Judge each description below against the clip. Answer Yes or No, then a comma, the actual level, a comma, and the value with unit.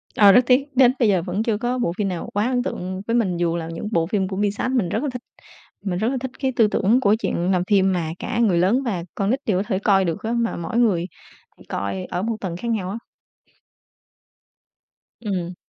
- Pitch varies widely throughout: No, average, 4.4 semitones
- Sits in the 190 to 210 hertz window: Yes, high, 205 Hz